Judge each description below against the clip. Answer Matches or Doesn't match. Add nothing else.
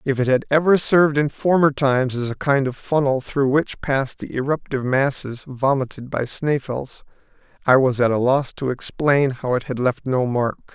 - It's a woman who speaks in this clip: Doesn't match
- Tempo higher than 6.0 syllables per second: Doesn't match